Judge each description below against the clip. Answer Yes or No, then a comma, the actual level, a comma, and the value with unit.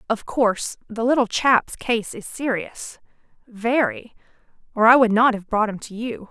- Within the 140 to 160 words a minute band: Yes, average, 150 wpm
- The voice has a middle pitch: No, high, 230 Hz